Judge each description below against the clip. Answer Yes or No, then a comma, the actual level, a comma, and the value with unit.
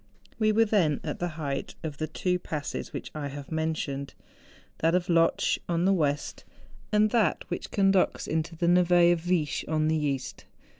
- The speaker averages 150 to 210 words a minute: Yes, average, 180 wpm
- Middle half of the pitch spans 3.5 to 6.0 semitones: No, average, 3.0 semitones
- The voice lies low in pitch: No, medium, 165 Hz